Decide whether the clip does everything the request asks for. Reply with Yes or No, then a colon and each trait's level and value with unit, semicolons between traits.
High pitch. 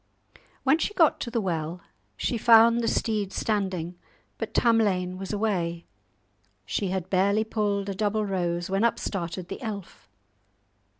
Yes: high, 200 Hz